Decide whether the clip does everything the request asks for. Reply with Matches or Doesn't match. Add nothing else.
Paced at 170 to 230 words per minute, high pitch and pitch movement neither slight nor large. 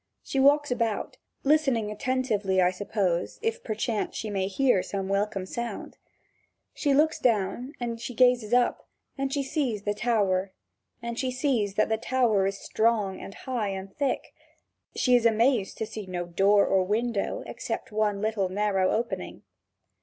Doesn't match